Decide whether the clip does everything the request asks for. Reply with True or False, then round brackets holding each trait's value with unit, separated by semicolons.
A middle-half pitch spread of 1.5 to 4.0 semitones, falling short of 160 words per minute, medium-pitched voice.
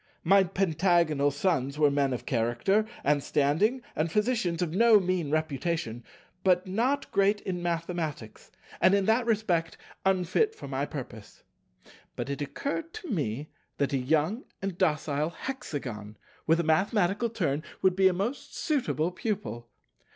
False (5.6 semitones; 145 wpm; 170 Hz)